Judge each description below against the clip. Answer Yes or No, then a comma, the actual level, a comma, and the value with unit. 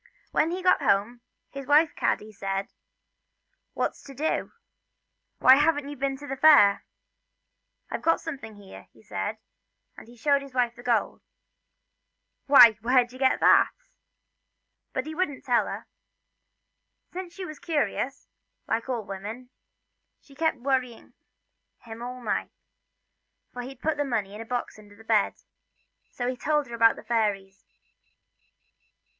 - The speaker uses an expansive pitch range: No, average, 4.3 semitones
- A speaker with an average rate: Yes, average, 160 wpm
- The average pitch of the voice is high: Yes, very high, 250 Hz